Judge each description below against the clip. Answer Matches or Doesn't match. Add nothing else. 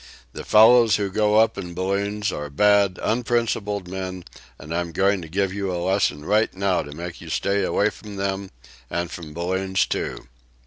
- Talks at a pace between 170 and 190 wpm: Matches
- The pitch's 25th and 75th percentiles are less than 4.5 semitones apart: Matches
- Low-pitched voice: Matches